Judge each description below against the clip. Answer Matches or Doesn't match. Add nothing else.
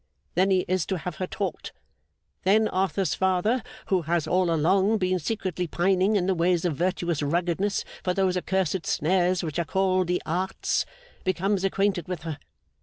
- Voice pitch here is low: Doesn't match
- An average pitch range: Doesn't match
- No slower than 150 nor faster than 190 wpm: Matches